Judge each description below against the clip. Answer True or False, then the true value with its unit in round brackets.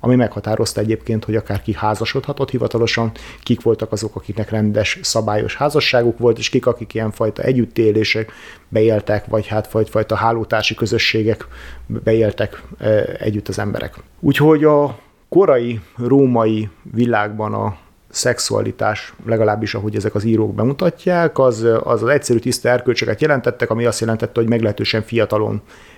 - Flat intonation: True (1.9 semitones)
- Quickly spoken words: False (130 wpm)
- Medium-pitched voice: False (110 Hz)